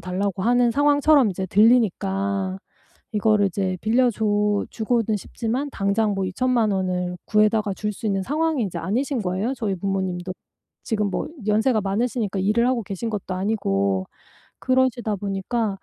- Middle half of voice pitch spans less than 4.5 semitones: Yes, average, 3.6 semitones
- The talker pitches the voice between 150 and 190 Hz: No, high, 210 Hz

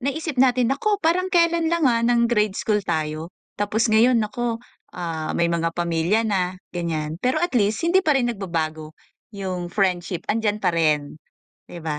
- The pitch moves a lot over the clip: Yes, wide, 6.8 semitones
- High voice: Yes, high, 205 Hz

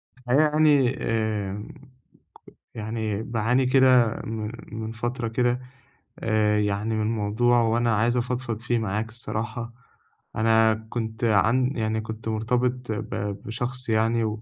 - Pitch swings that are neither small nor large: No, narrow, 1.9 semitones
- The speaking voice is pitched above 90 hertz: Yes, low, 115 Hz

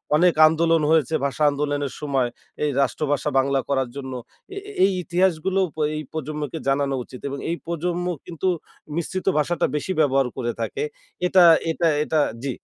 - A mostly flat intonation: No, average, 3.6 semitones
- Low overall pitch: No, medium, 150 Hz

